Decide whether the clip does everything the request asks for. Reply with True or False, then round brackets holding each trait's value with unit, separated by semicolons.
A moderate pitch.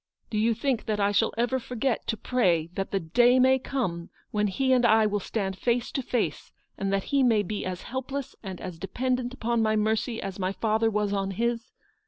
False (220 Hz)